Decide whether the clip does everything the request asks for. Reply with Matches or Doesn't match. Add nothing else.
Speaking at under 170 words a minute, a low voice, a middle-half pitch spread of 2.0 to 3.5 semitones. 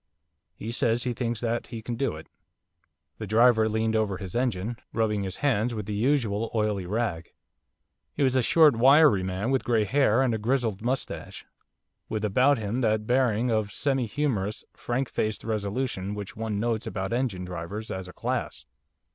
Doesn't match